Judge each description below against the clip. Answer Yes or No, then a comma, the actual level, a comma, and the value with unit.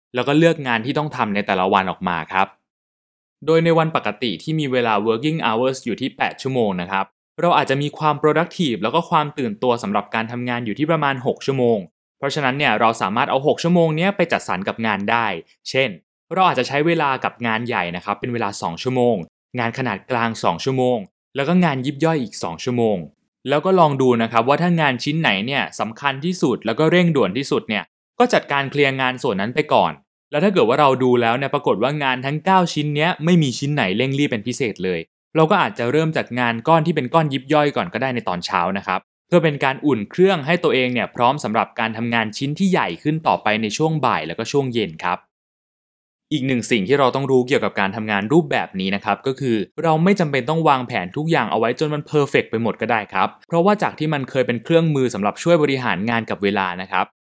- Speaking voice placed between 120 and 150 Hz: Yes, low, 135 Hz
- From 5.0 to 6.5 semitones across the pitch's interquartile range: Yes, average, 5.3 semitones